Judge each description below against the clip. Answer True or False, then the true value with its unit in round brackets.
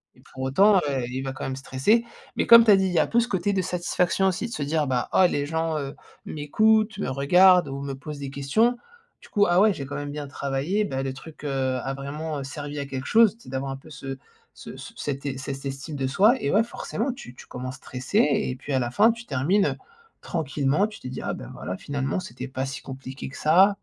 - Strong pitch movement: True (6.1 semitones)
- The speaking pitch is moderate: True (145 Hz)